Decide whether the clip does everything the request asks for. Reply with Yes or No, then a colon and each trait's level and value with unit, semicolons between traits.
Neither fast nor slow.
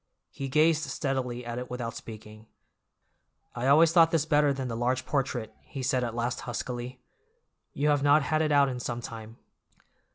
Yes: average, 175 wpm